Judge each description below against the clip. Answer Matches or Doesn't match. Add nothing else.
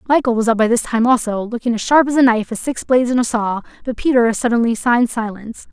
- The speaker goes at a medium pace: Doesn't match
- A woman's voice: Matches